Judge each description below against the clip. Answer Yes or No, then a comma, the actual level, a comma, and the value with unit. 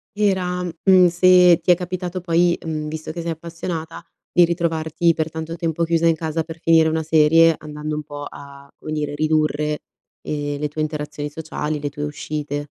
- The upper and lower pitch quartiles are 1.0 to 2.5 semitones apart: Yes, narrow, 2.0 semitones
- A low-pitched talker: No, medium, 160 Hz